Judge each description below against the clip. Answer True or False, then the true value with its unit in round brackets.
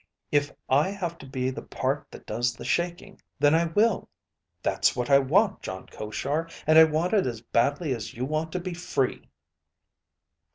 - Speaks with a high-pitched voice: False (145 Hz)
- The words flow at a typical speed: True (180 wpm)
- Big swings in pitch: False (4.8 semitones)